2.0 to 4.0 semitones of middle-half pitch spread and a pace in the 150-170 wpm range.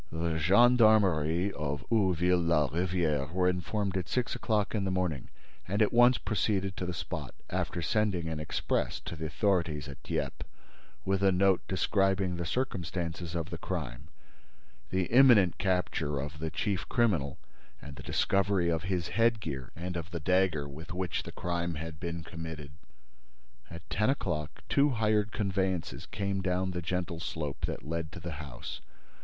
Yes: average, 3.4 semitones; average, 160 wpm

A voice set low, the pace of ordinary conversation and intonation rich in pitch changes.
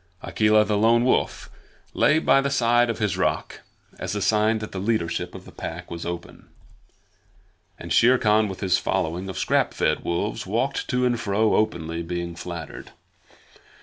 No: low, 105 Hz; average, 170 wpm; average, 4.6 semitones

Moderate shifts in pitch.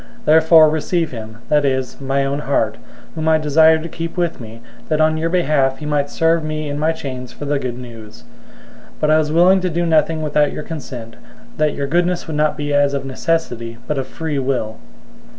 Yes: average, 3.1 semitones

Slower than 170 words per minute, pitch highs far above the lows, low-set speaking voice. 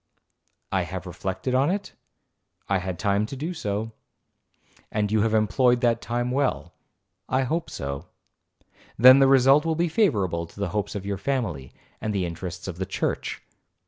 Yes: average, 150 wpm; wide, 5.8 semitones; low, 110 Hz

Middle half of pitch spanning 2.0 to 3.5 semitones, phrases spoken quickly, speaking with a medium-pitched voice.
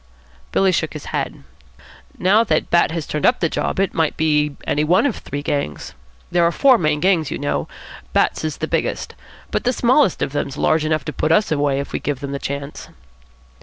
No: average, 4.1 semitones; fast, 210 wpm; medium, 155 Hz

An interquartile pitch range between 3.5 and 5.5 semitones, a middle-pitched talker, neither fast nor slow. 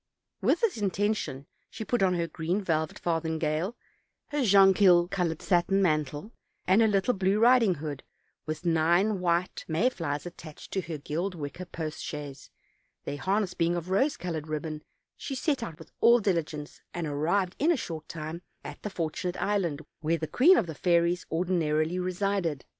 Yes: average, 3.9 semitones; medium, 175 Hz; average, 175 wpm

